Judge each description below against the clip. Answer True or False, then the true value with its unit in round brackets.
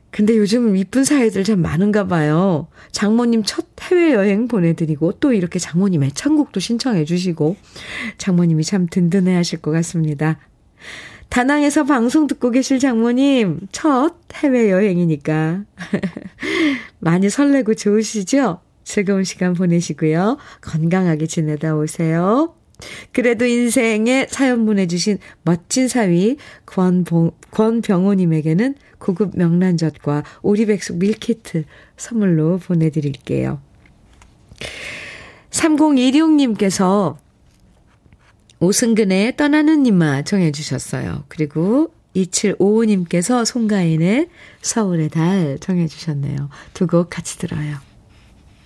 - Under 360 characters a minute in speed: True (250 characters per minute)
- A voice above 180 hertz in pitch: True (190 Hz)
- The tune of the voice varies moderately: False (6.4 semitones)